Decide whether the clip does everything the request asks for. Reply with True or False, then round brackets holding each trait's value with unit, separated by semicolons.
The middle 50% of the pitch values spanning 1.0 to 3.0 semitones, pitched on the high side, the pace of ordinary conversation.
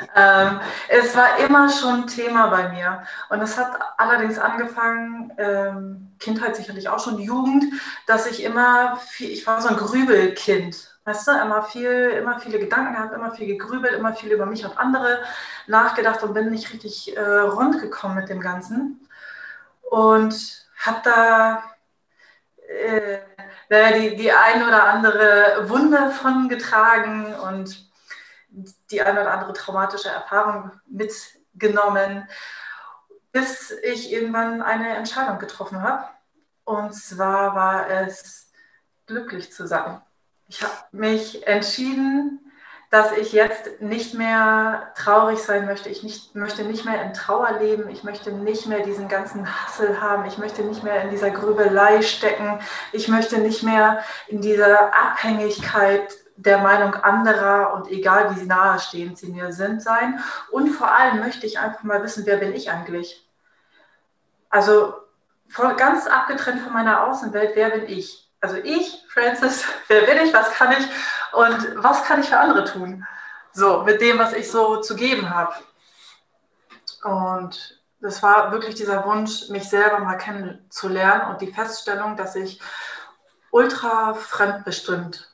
True (2.5 semitones; 215 Hz; 145 wpm)